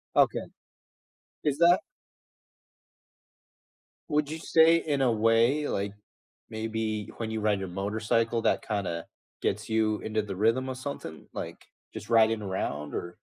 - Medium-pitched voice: No, low, 110 Hz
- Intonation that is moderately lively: Yes, average, 3.9 semitones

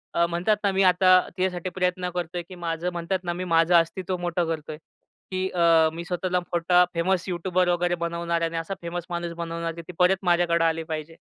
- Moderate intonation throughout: No, narrow, 1.3 semitones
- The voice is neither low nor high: Yes, medium, 175 Hz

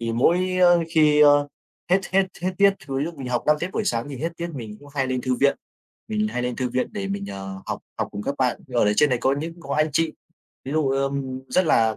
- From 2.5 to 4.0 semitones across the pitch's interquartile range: No, average, 5.2 semitones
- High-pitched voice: No, medium, 140 Hz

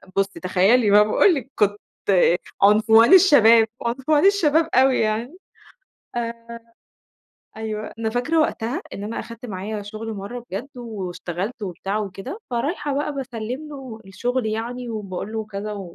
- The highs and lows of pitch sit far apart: No, average, 3.6 semitones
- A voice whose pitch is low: No, high, 225 Hz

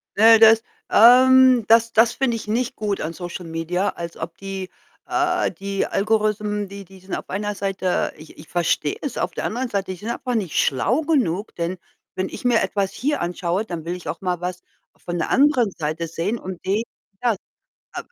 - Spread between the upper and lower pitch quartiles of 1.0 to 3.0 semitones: No, average, 4.4 semitones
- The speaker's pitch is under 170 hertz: No, high, 200 Hz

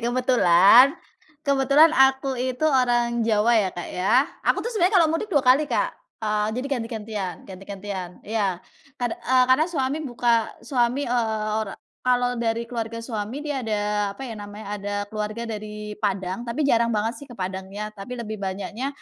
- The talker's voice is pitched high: Yes, high, 235 Hz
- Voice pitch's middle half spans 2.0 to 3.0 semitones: No, average, 3.7 semitones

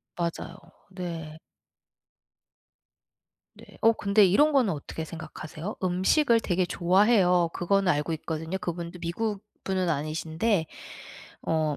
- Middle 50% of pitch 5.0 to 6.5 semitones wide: No, average, 3.6 semitones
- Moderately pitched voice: Yes, medium, 175 Hz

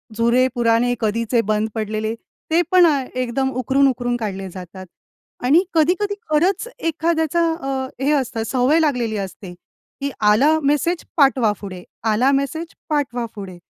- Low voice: No, very high, 255 Hz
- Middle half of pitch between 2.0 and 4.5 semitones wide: No, average, 5.2 semitones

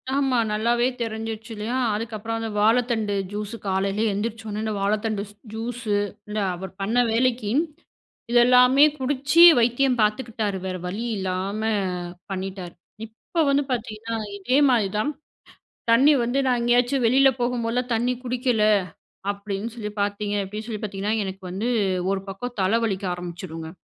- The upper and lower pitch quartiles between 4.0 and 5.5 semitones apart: No, average, 3.2 semitones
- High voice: Yes, high, 225 Hz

